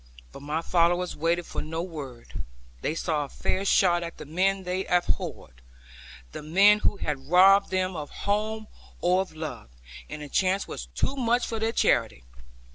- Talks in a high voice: No, medium, 175 Hz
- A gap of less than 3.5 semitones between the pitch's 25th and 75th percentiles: No, average, 4.2 semitones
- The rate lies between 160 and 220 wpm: Yes, average, 175 wpm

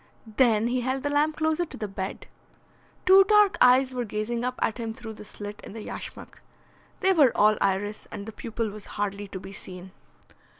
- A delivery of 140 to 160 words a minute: No, average, 200 wpm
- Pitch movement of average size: Yes, average, 4.2 semitones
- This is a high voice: Yes, high, 225 Hz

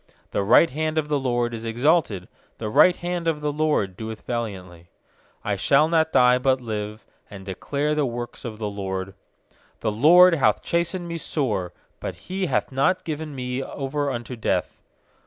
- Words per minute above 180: No, average, 175 wpm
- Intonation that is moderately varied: No, wide, 6.3 semitones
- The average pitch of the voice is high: No, low, 130 Hz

